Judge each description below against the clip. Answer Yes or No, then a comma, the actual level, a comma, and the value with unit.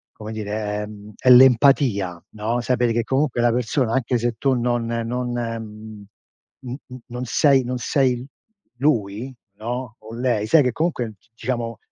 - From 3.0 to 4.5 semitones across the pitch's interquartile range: No, narrow, 2.4 semitones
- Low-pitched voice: Yes, low, 120 Hz